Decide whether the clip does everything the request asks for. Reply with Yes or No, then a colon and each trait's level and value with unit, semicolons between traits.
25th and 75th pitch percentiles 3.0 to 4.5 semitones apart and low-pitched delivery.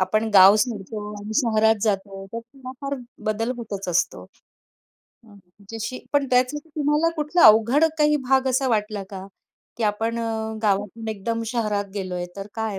No: average, 3.7 semitones; high, 225 Hz